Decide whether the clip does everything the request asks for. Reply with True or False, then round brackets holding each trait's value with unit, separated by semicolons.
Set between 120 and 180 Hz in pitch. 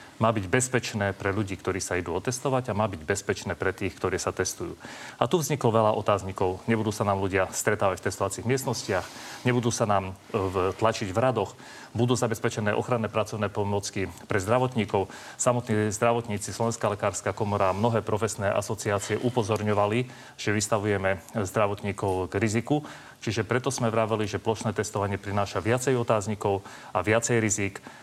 False (110 Hz)